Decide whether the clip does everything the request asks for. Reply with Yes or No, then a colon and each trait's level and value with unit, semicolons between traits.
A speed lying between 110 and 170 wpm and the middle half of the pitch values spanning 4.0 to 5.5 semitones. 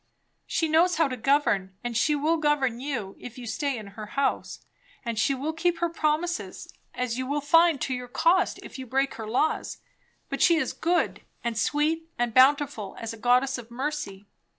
No: average, 195 wpm; average, 4.7 semitones